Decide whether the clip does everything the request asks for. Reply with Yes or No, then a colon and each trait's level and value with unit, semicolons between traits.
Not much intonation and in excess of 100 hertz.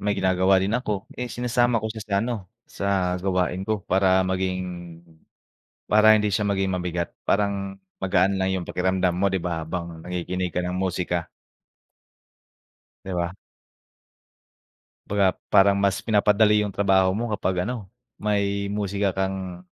No: narrow, 1.8 semitones; very low, 95 Hz